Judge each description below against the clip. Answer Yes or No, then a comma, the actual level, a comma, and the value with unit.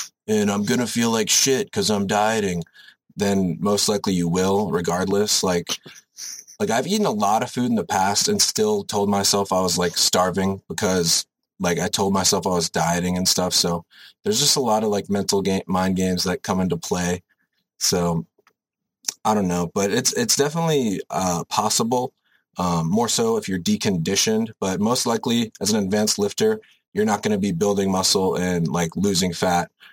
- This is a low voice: Yes, low, 100 Hz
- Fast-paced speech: No, average, 185 wpm